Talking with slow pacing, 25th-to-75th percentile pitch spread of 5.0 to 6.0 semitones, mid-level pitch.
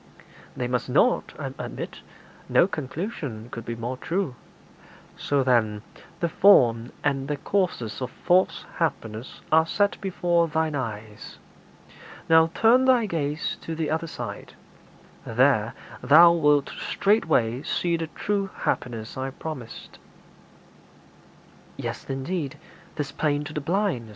Yes: slow, 125 wpm; wide, 5.4 semitones; medium, 150 Hz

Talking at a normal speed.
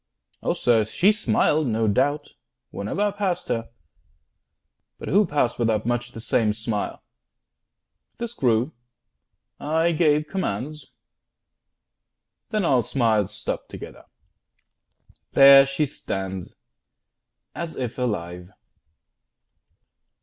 No: slow, 100 wpm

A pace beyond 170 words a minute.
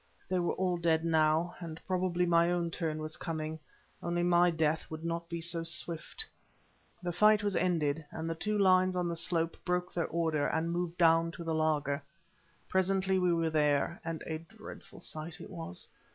Yes: average, 185 wpm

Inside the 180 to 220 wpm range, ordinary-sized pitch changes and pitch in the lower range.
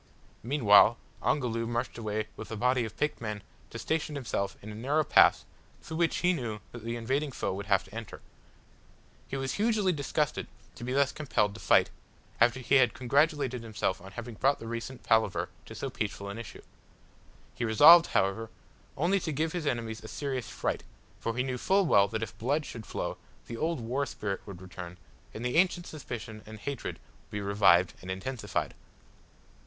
Yes: average, 185 wpm; average, 4.8 semitones; low, 120 Hz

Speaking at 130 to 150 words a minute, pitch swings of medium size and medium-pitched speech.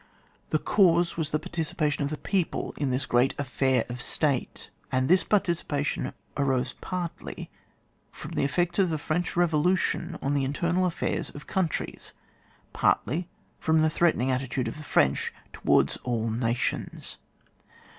Yes: average, 145 wpm; average, 4.6 semitones; medium, 150 Hz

